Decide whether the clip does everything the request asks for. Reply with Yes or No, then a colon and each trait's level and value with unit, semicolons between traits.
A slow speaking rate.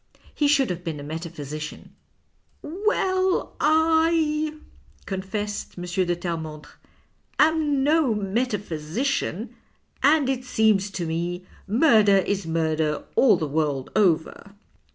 Yes: slow, 115 wpm